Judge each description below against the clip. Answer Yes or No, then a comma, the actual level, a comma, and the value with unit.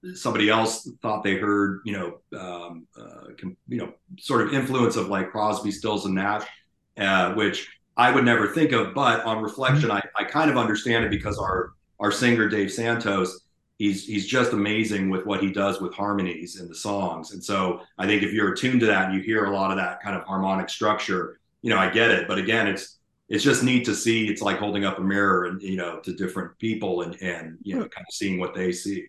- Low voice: Yes, low, 100 Hz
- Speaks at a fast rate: Yes, fast, 225 wpm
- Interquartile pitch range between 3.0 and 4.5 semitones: No, narrow, 2.5 semitones